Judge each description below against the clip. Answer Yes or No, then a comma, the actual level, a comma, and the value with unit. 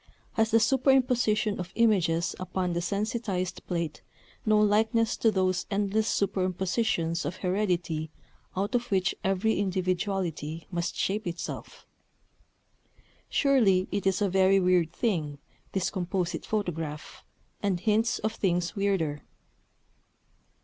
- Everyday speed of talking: No, slow, 115 wpm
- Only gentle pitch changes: No, average, 3.4 semitones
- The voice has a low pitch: No, high, 190 Hz